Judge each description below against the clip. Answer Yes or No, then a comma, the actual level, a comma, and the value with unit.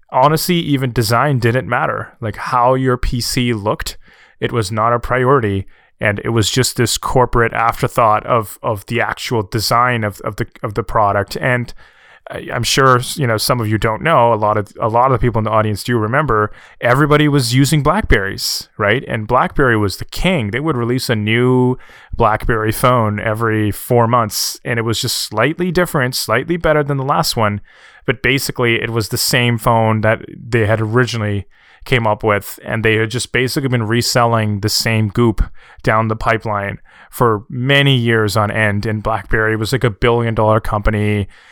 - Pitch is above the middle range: No, low, 115 Hz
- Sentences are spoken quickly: No, average, 185 wpm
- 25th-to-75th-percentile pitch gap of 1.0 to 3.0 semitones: Yes, narrow, 2.6 semitones